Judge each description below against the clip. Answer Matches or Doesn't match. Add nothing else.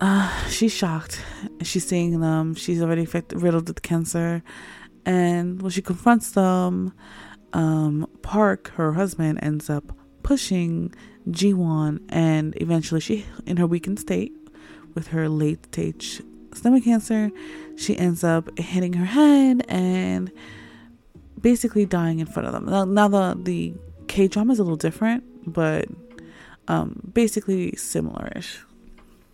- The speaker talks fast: Doesn't match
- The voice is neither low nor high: Matches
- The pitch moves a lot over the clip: Doesn't match